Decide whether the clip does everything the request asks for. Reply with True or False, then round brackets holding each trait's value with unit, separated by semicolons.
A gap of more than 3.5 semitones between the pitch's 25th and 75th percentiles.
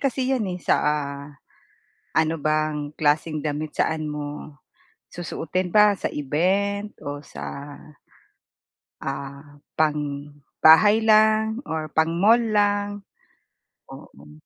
True (5.6 semitones)